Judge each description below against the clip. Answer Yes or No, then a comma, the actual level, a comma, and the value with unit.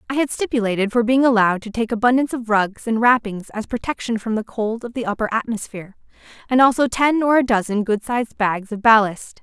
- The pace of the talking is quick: Yes, fast, 210 wpm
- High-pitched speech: Yes, high, 230 Hz